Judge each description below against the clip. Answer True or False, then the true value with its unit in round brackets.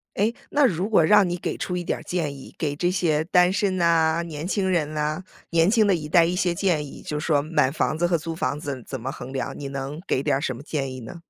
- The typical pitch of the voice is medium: True (160 Hz)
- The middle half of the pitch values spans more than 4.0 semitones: False (3.5 semitones)